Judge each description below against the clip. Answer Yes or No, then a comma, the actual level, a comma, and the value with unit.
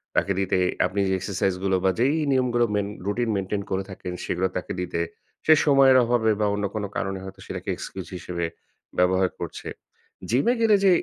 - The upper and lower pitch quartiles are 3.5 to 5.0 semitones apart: Yes, average, 4.2 semitones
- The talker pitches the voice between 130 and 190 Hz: No, low, 100 Hz